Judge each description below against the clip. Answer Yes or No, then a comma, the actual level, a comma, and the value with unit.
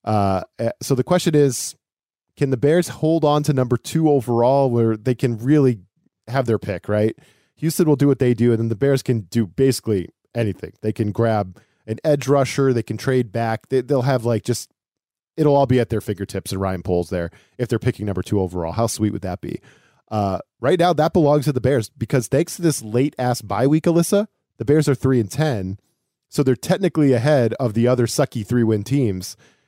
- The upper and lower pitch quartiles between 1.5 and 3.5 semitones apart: No, average, 4.6 semitones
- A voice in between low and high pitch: No, low, 125 Hz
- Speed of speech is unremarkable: No, fast, 215 wpm